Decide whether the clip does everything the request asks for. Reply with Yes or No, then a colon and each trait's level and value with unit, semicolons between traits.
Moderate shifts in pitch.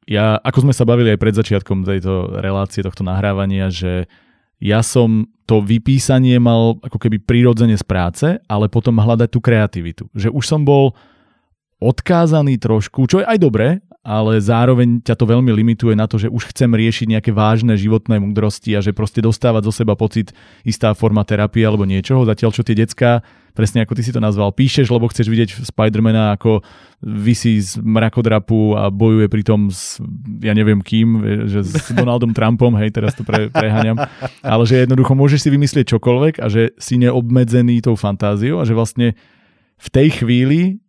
No: narrow, 2.3 semitones